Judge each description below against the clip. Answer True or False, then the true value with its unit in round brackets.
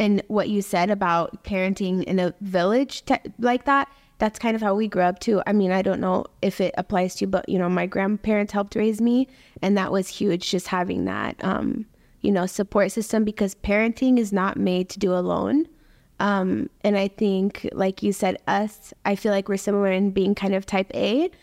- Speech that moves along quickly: True (215 wpm)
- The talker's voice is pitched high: True (200 Hz)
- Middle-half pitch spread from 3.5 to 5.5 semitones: False (2.4 semitones)